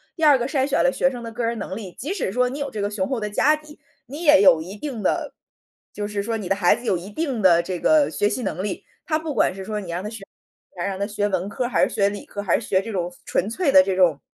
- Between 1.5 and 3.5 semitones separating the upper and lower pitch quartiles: No, wide, 5.6 semitones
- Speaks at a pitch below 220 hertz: Yes, high, 210 Hz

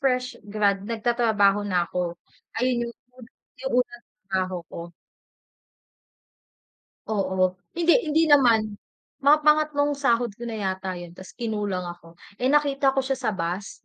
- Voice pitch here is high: Yes, high, 225 Hz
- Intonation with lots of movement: Yes, wide, 6.0 semitones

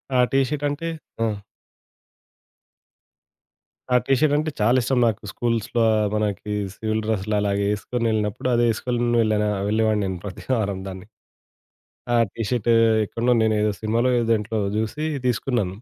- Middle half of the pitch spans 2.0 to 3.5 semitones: Yes, narrow, 2.4 semitones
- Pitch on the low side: Yes, low, 110 Hz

